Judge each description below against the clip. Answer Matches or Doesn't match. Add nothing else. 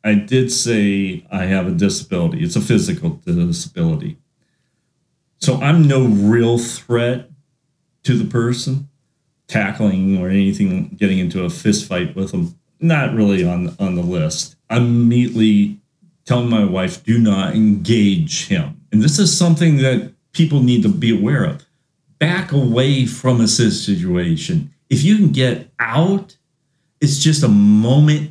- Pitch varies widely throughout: Matches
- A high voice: Doesn't match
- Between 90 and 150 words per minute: Matches